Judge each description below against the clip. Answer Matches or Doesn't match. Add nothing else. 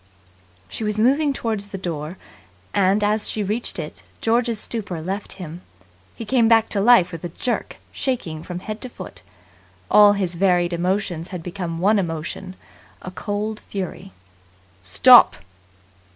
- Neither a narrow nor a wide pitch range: Matches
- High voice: Matches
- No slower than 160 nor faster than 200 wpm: Doesn't match